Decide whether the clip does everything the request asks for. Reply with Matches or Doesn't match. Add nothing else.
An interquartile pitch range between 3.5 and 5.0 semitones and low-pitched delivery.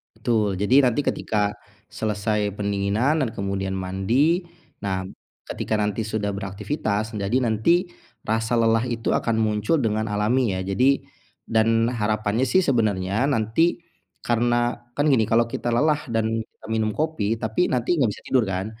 Doesn't match